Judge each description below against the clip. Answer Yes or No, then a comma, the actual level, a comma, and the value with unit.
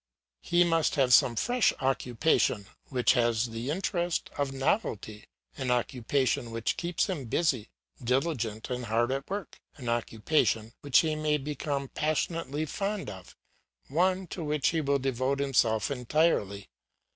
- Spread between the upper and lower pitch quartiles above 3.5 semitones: Yes, average, 4.9 semitones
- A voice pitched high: No, low, 135 Hz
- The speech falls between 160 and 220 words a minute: No, average, 140 wpm